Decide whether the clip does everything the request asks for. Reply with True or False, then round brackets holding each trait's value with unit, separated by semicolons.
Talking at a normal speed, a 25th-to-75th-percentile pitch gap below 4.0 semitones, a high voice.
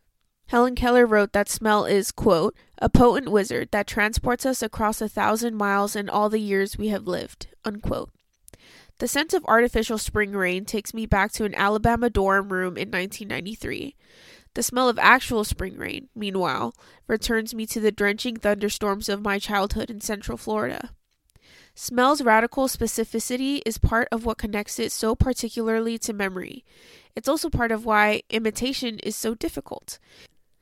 True (160 wpm; 2.5 semitones; 220 Hz)